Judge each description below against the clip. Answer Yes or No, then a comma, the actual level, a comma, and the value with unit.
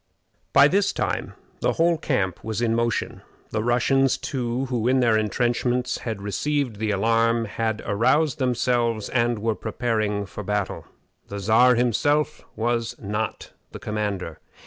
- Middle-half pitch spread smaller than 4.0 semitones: Yes, average, 2.7 semitones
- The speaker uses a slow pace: No, average, 145 wpm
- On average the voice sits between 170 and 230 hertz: No, low, 115 Hz